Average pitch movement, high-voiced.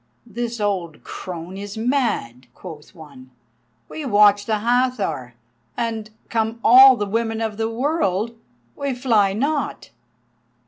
Yes: average, 3.8 semitones; high, 220 Hz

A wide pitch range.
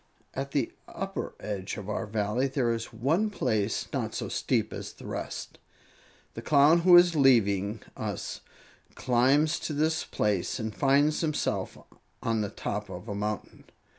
Yes: wide, 5.8 semitones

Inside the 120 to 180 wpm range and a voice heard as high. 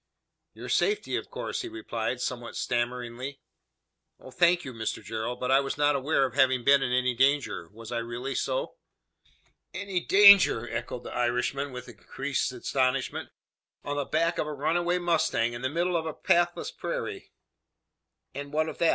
No: average, 170 wpm; low, 135 Hz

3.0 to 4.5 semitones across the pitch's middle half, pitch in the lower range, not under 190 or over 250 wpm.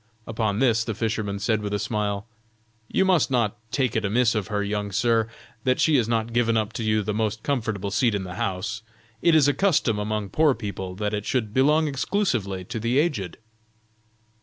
Yes: average, 3.3 semitones; low, 110 Hz; average, 200 wpm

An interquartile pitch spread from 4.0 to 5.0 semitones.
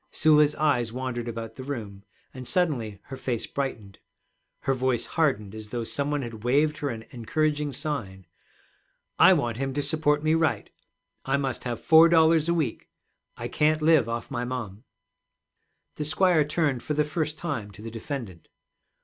Yes: average, 4.7 semitones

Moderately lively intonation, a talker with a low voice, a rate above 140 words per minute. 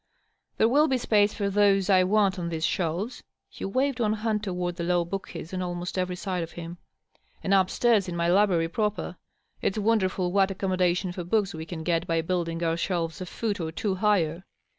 No: average, 3.0 semitones; medium, 185 Hz; fast, 205 wpm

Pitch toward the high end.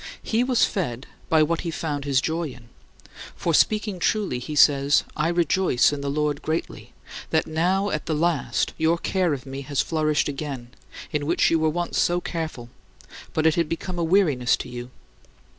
No: medium, 155 Hz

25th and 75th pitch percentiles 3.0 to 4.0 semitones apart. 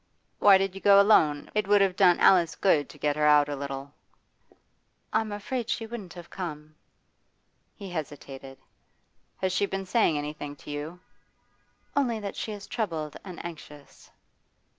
No: average, 5.3 semitones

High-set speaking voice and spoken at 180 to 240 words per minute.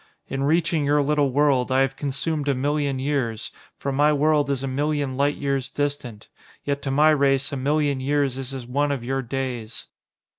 No: medium, 140 Hz; average, 190 wpm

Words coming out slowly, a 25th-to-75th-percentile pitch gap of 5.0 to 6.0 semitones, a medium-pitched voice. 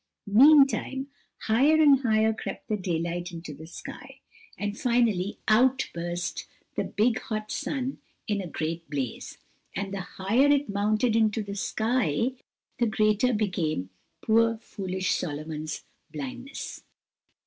No: slow, 125 wpm; wide, 5.4 semitones; high, 210 Hz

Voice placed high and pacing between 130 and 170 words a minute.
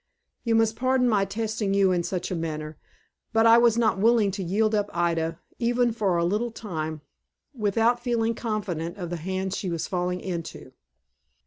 No: high, 200 Hz; average, 180 wpm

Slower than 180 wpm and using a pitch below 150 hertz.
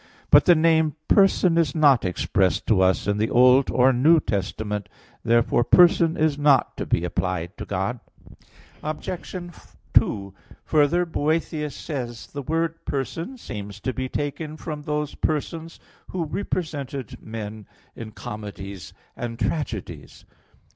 Yes: average, 140 wpm; medium, 140 Hz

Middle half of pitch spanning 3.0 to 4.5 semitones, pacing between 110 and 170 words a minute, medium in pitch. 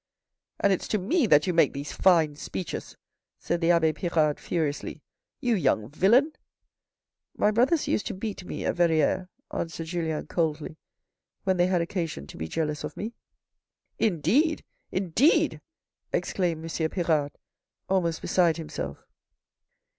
Yes: average, 3.6 semitones; average, 155 wpm; medium, 170 Hz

